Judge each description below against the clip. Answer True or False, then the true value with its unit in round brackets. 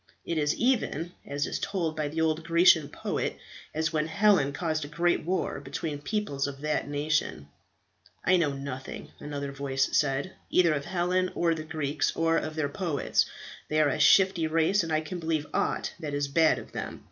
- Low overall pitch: False (155 Hz)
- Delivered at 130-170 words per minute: False (190 wpm)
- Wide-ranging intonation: False (2.9 semitones)